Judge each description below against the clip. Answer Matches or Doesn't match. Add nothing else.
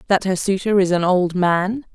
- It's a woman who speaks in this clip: Matches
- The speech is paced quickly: Matches